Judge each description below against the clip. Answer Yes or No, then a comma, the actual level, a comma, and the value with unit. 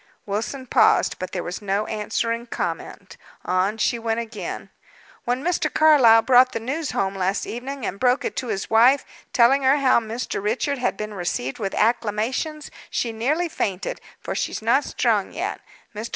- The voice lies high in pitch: Yes, high, 230 Hz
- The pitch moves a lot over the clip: No, average, 3.8 semitones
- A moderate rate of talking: Yes, average, 170 wpm